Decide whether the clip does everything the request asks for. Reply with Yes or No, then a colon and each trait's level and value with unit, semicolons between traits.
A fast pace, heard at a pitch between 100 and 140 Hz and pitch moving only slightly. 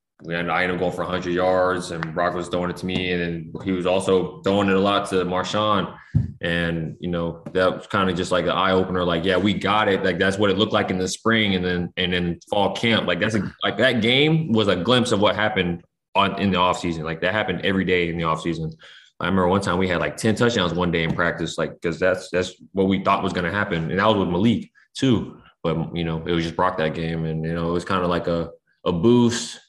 No: fast, 270 wpm; very low, 90 Hz; narrow, 2.1 semitones